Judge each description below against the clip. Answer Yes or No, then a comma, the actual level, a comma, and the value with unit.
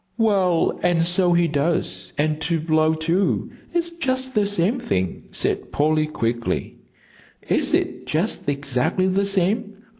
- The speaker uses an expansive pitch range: No, average, 4.7 semitones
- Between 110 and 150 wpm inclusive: Yes, average, 140 wpm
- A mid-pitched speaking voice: Yes, medium, 170 Hz